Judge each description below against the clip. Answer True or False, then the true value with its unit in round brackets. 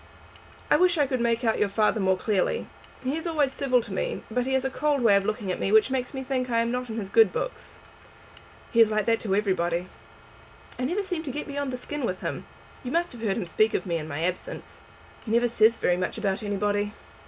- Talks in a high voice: True (230 Hz)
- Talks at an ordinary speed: False (245 wpm)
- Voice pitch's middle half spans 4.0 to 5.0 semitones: True (4.7 semitones)